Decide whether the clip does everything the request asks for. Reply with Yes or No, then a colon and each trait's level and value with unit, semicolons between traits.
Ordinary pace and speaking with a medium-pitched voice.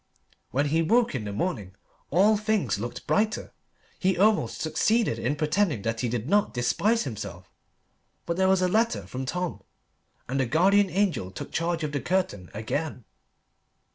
Yes: average, 165 wpm; medium, 160 Hz